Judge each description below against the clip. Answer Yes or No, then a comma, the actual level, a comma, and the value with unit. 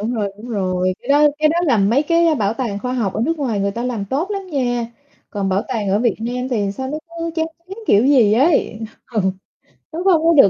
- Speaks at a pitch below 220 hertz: No, high, 245 Hz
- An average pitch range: No, wide, 6.5 semitones